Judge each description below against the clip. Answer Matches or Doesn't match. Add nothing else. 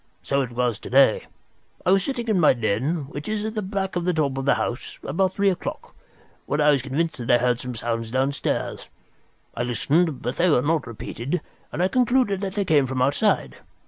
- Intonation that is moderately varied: Doesn't match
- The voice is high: Doesn't match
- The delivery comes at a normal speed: Doesn't match